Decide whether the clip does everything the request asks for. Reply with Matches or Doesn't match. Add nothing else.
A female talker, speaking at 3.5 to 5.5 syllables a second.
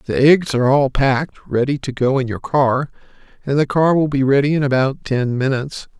Matches